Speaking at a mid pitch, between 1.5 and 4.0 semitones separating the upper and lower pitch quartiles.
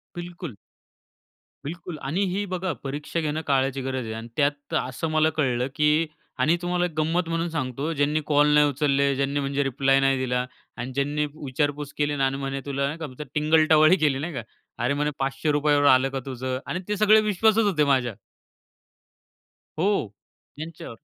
Yes: medium, 145 Hz; average, 2.9 semitones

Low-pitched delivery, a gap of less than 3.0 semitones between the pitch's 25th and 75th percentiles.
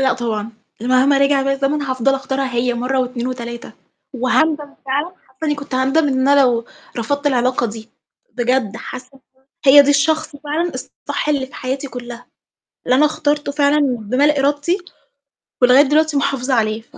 No: very high, 270 Hz; narrow, 2.5 semitones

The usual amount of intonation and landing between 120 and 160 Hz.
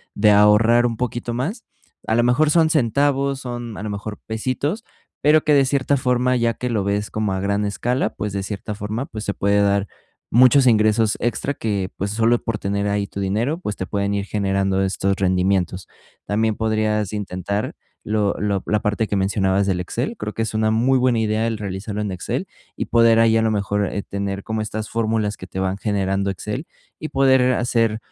No: average, 3.0 semitones; low, 105 Hz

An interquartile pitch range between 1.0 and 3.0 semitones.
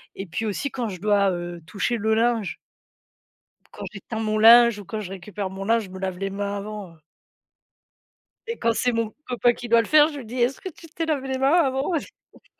No: average, 3.8 semitones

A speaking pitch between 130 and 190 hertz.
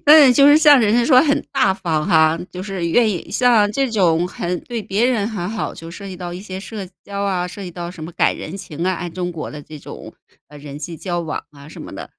Yes: medium, 185 Hz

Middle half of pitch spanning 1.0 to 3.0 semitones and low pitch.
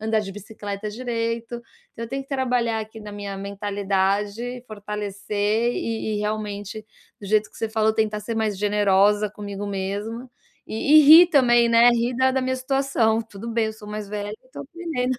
No: narrow, 2.6 semitones; high, 220 Hz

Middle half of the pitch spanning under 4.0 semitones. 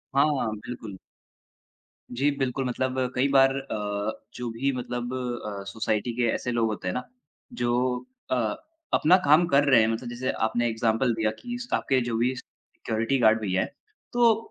Yes: average, 3.2 semitones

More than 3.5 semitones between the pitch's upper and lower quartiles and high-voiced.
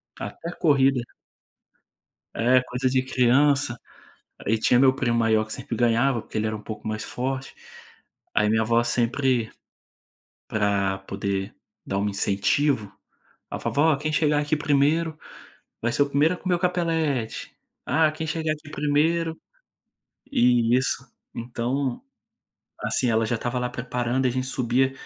No: average, 4.2 semitones; low, 125 Hz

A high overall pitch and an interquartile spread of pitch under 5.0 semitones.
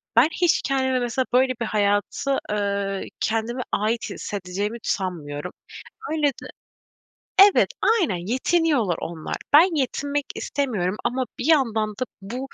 No: high, 235 Hz; average, 5.3 semitones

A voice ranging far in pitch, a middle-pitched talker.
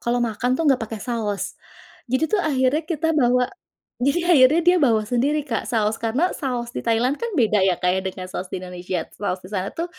No: wide, 5.9 semitones; high, 245 Hz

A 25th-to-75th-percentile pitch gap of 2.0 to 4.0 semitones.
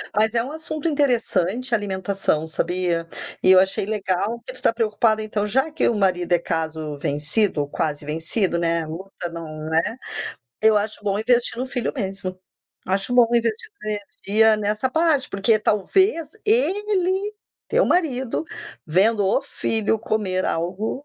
No: average, 5.2 semitones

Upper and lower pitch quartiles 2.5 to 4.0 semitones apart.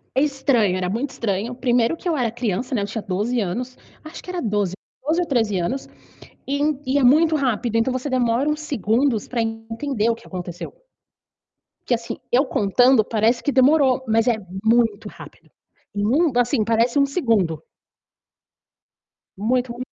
Yes: average, 3.5 semitones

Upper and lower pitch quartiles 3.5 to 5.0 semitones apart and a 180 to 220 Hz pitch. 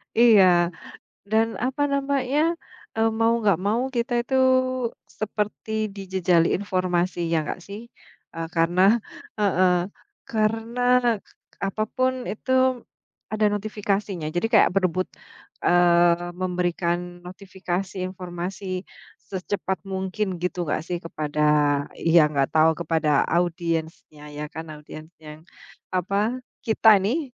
Yes: average, 4.2 semitones; medium, 185 Hz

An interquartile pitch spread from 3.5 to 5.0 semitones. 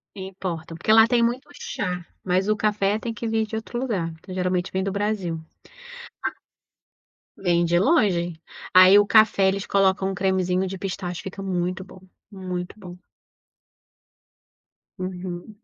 No: narrow, 2.6 semitones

